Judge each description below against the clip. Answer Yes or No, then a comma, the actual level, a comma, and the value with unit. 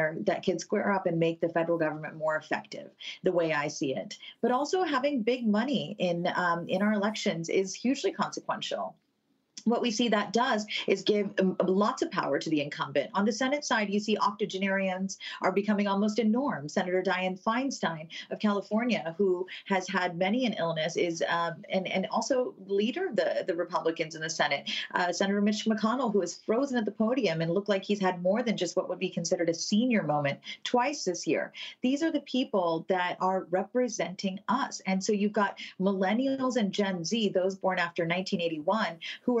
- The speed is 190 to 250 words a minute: Yes, average, 195 wpm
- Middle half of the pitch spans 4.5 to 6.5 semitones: No, average, 3.9 semitones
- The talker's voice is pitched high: Yes, high, 195 Hz